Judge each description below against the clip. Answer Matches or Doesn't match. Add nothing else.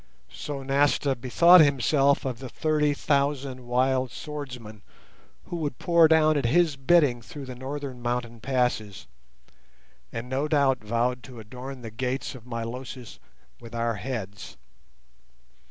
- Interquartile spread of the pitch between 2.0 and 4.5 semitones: Matches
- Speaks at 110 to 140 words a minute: Matches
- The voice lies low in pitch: Matches